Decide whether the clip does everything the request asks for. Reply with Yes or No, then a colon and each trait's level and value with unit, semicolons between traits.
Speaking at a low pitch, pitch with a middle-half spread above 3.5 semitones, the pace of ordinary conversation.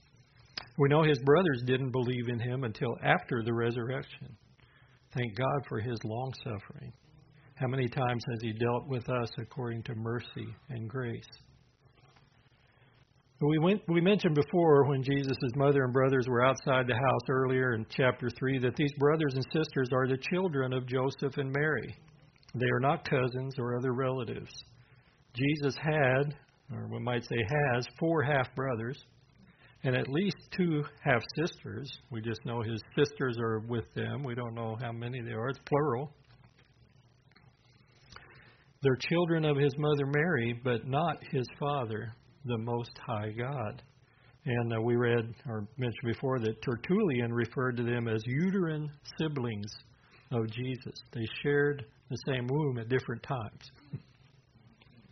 No: low, 130 Hz; average, 2.9 semitones; average, 150 wpm